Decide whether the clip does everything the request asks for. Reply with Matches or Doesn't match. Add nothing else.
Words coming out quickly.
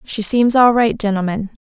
Doesn't match